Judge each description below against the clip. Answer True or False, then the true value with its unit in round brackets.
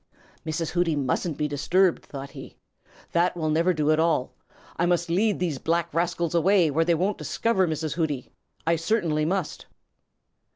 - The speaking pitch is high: False (165 Hz)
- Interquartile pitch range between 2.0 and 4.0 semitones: True (2.4 semitones)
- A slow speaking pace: False (165 wpm)